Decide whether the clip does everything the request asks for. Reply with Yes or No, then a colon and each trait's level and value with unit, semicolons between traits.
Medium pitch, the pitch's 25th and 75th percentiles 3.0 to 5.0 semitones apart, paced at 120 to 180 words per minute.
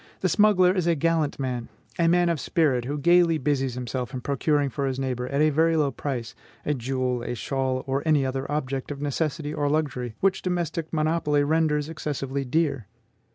No: medium, 145 Hz; average, 3.5 semitones; average, 190 wpm